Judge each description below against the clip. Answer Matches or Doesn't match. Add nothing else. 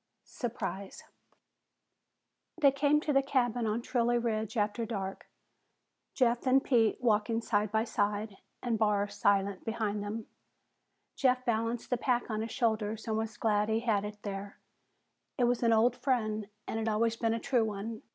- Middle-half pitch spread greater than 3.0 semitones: Doesn't match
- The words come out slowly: Doesn't match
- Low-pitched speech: Doesn't match